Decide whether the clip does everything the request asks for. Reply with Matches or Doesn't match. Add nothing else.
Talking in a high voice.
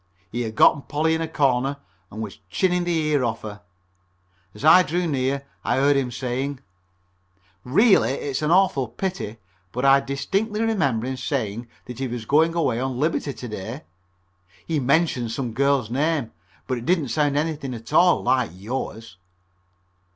Doesn't match